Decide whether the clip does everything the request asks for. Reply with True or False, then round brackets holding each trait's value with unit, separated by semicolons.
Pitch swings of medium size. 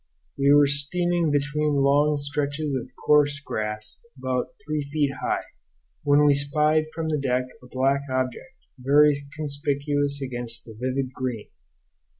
False (2.3 semitones)